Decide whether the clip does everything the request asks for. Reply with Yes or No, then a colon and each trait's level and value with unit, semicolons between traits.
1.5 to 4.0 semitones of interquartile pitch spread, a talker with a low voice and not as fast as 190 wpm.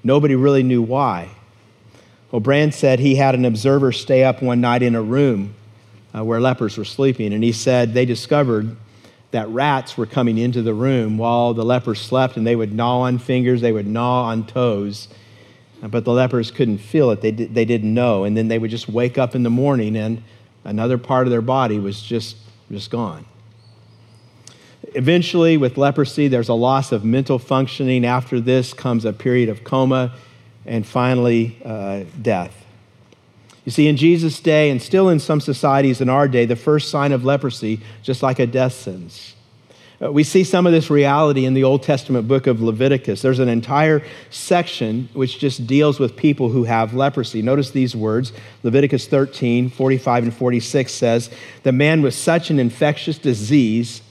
Yes: average, 2.9 semitones; low, 125 Hz; average, 180 wpm